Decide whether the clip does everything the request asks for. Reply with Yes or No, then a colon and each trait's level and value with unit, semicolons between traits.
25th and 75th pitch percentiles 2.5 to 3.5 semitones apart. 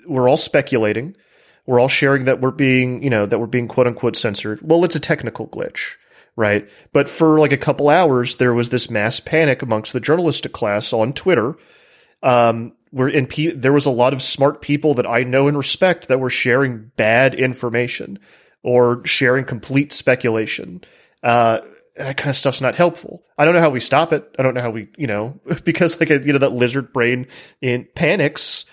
Yes: average, 3.2 semitones